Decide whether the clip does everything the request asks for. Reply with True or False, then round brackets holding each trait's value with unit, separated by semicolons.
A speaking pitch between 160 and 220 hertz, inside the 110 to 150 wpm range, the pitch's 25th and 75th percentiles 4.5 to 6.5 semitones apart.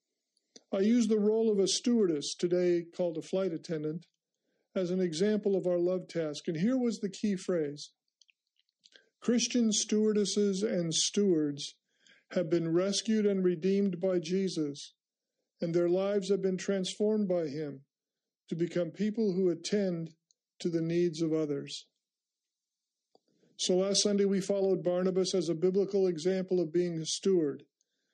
False (185 Hz; 145 wpm; 2.9 semitones)